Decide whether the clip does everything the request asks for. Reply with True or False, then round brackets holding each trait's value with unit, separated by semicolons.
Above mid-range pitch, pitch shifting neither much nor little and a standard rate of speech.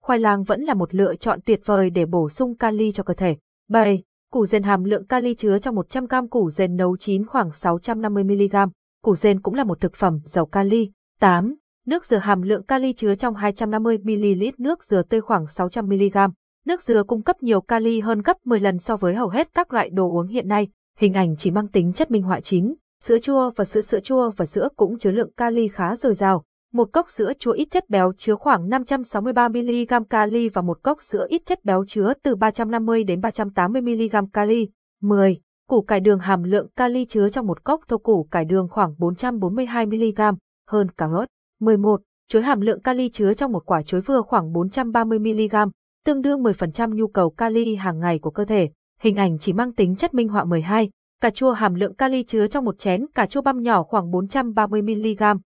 True (215 Hz; 3.5 semitones; 210 wpm)